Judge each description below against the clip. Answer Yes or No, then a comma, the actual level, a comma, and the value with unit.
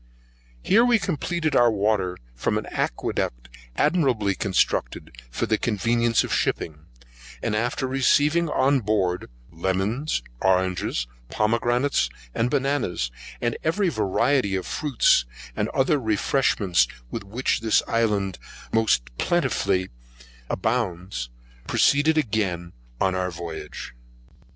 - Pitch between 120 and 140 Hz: No, low, 110 Hz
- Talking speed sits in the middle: No, slow, 110 wpm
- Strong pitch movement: Yes, wide, 6.5 semitones